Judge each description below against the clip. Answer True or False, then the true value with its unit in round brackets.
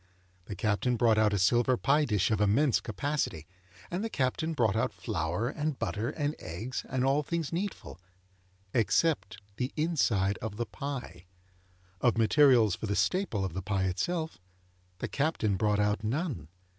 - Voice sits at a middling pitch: False (115 Hz)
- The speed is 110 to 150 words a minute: False (160 wpm)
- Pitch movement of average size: False (6.2 semitones)